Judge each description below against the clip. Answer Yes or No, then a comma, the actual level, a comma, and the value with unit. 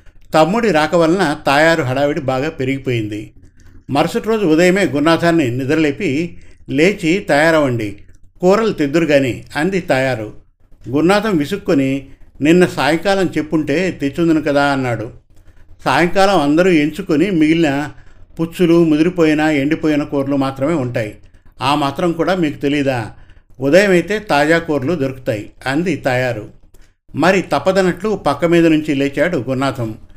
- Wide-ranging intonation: No, average, 5.0 semitones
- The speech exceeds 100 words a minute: Yes, average, 110 wpm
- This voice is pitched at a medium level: Yes, medium, 145 Hz